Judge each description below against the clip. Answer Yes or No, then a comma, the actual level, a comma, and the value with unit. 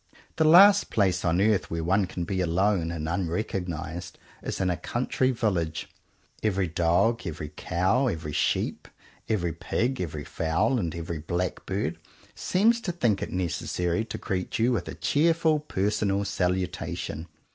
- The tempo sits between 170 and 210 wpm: No, average, 145 wpm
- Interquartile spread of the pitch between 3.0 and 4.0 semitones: No, average, 4.9 semitones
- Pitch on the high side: No, very low, 95 Hz